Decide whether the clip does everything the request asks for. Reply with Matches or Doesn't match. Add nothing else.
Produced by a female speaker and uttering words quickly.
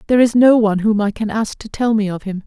Matches